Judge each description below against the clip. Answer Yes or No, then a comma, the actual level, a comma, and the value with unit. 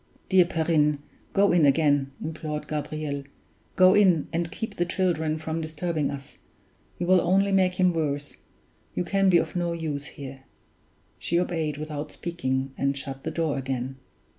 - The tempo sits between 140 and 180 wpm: Yes, average, 160 wpm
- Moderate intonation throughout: Yes, average, 3.5 semitones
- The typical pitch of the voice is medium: Yes, medium, 160 Hz